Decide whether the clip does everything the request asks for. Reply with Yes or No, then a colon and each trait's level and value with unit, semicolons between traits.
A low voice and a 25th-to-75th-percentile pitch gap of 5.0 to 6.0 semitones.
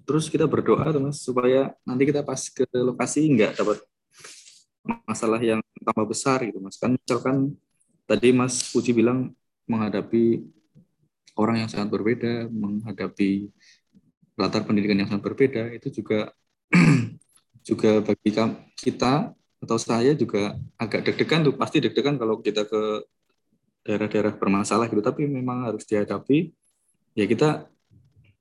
No: low, 115 Hz; average, 3.8 semitones